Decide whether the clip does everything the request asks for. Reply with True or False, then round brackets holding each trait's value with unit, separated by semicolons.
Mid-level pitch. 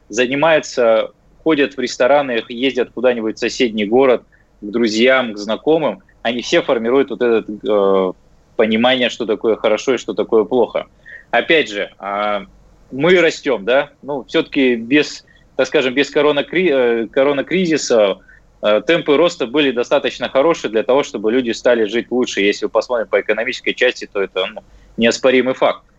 False (125 Hz)